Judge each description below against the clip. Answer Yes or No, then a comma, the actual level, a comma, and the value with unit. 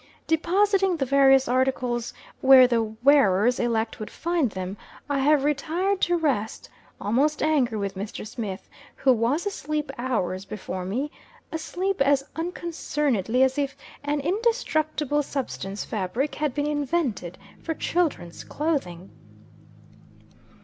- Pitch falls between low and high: No, very high, 275 Hz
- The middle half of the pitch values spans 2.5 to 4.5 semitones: No, wide, 5.5 semitones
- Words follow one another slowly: Yes, slow, 120 wpm